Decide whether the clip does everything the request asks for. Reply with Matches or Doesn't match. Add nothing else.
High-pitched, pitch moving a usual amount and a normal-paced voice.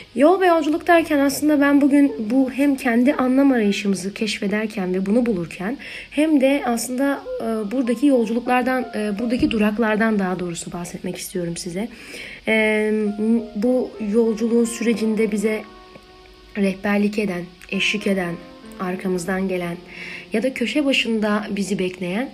Matches